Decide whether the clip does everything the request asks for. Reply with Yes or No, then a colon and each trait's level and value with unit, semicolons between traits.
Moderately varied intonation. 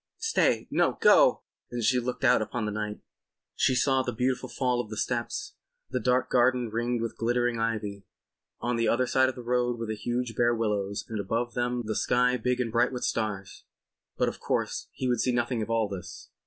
No: narrow, 2.1 semitones